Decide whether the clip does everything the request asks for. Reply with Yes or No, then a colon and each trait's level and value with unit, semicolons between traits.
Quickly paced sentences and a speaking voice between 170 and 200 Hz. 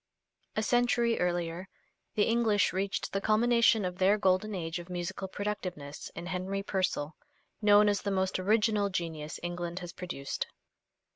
No: average, 145 wpm; high, 190 Hz